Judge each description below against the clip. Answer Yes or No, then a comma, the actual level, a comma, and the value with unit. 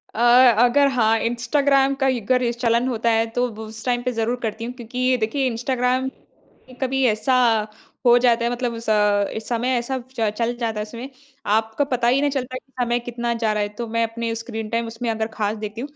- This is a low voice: No, high, 235 Hz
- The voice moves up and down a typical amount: No, narrow, 2.0 semitones